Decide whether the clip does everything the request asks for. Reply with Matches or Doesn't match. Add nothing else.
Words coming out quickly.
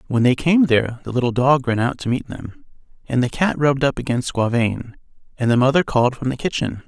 Matches